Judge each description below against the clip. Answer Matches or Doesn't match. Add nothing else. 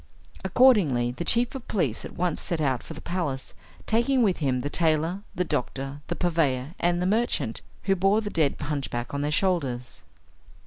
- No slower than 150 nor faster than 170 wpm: Doesn't match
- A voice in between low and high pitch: Matches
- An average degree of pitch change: Doesn't match